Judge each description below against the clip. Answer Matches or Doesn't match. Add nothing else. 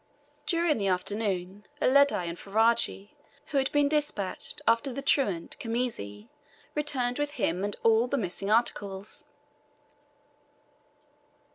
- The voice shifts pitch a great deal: Matches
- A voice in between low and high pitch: Doesn't match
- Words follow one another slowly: Matches